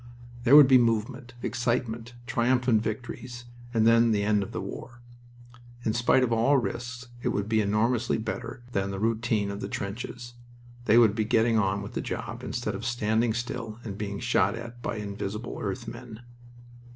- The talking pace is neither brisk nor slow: Yes, average, 175 wpm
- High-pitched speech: No, low, 115 Hz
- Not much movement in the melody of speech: Yes, narrow, 2.2 semitones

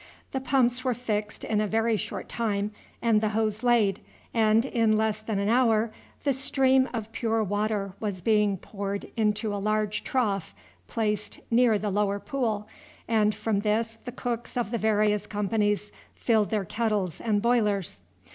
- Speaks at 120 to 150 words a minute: No, average, 165 wpm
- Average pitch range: No, narrow, 1.9 semitones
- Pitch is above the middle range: Yes, high, 215 Hz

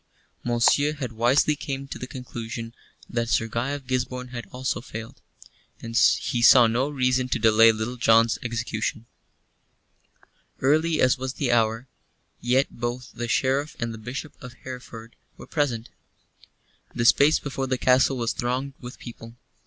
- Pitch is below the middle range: Yes, low, 125 Hz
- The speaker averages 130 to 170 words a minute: Yes, average, 155 wpm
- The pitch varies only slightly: Yes, narrow, 2.3 semitones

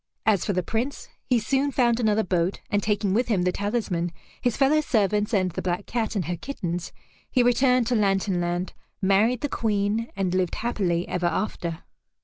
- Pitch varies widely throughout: No, average, 4.5 semitones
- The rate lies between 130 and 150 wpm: No, average, 185 wpm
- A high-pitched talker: Yes, high, 205 Hz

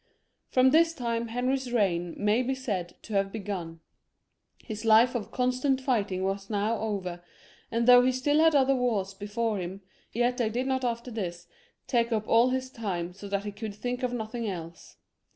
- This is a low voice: No, high, 225 Hz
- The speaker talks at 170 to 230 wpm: Yes, average, 190 wpm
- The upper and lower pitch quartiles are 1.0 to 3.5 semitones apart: No, average, 4.0 semitones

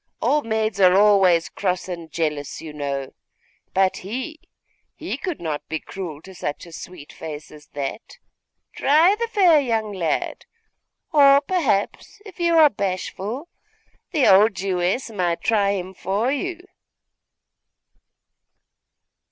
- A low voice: No, high, 195 Hz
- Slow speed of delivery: Yes, slow, 130 wpm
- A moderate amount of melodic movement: No, wide, 8.3 semitones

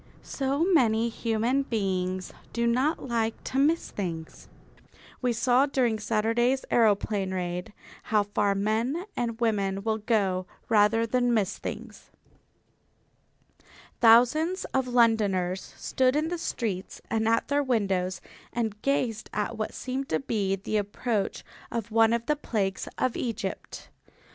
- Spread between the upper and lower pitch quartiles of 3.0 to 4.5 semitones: Yes, average, 3.5 semitones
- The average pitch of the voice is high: Yes, high, 225 Hz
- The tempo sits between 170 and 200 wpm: No, slow, 135 wpm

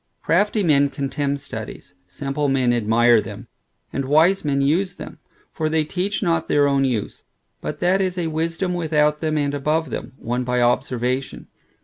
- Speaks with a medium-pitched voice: Yes, medium, 145 Hz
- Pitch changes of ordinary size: Yes, average, 4.0 semitones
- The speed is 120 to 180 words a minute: Yes, average, 165 wpm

